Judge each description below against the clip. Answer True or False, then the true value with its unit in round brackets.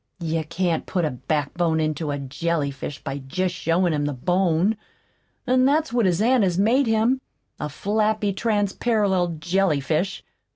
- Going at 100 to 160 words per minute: True (150 wpm)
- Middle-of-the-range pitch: True (175 Hz)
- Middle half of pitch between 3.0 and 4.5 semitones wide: False (5.2 semitones)